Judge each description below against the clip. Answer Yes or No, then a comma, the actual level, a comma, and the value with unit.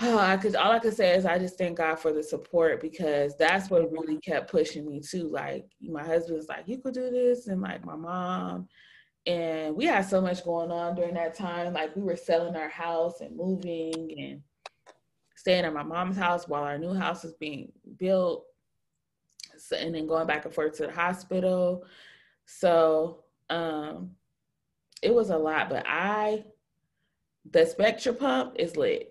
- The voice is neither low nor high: Yes, medium, 175 Hz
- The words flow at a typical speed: Yes, average, 185 wpm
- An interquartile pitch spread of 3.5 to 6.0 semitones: No, average, 3.0 semitones